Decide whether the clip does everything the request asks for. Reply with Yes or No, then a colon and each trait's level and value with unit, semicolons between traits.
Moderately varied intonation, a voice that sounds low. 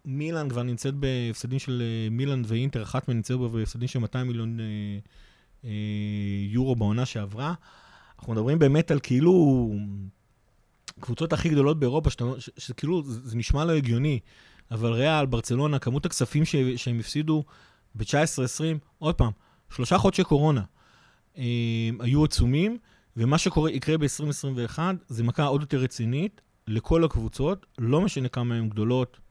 Yes: average, 4.5 semitones; low, 125 Hz